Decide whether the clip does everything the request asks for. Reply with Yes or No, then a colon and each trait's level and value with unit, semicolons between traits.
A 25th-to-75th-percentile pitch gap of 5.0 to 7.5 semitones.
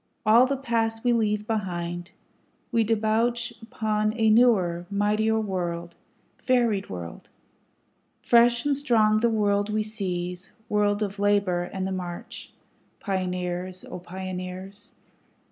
No: average, 3.5 semitones